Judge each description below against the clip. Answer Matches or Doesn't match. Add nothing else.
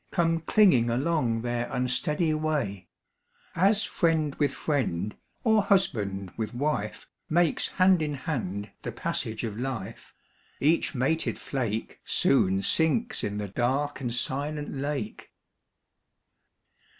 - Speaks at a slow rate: Matches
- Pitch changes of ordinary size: Doesn't match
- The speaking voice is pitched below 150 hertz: Matches